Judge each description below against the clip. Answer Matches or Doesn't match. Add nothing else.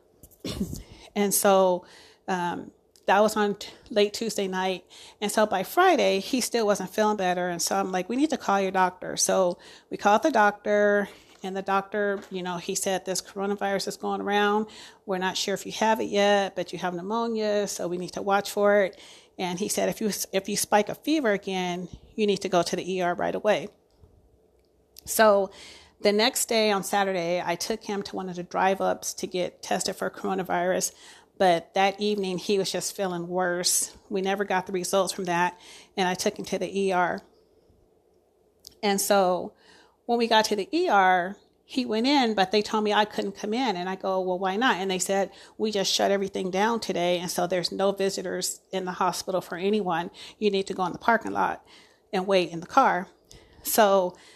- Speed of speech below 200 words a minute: Doesn't match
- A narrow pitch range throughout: Matches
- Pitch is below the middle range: Doesn't match